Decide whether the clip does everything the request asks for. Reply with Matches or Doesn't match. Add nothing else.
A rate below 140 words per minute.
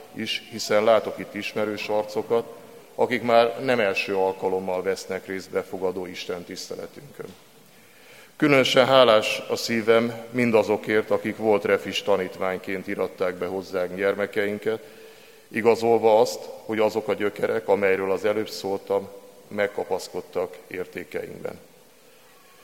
Matches